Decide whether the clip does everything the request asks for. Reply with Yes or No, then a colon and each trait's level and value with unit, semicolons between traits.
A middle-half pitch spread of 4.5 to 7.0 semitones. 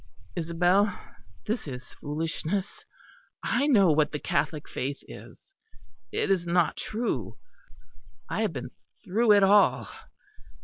Yes: average, 5.2 semitones